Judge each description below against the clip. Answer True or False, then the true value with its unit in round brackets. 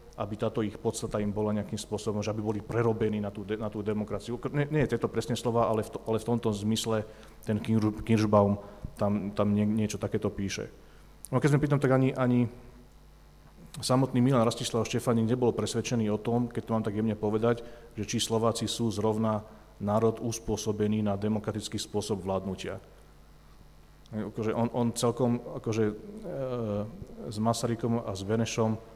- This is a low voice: True (110 Hz)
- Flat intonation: True (1.9 semitones)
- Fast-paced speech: True (170 wpm)